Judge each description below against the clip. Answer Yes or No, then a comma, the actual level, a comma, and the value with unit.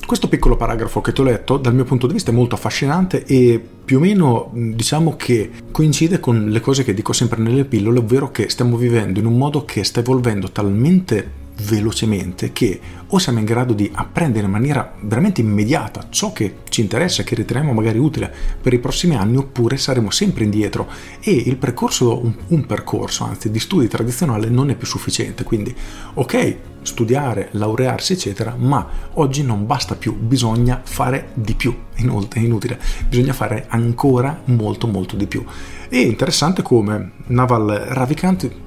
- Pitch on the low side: Yes, low, 120 Hz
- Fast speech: Yes, fast, 175 wpm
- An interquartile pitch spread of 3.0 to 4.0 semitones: Yes, average, 3.7 semitones